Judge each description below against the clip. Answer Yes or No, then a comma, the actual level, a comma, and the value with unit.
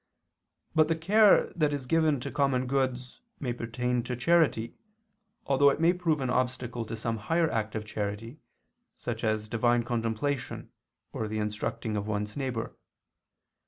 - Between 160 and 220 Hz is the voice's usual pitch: No, low, 125 Hz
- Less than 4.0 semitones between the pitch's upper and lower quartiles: No, average, 4.3 semitones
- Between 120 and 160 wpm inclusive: Yes, average, 155 wpm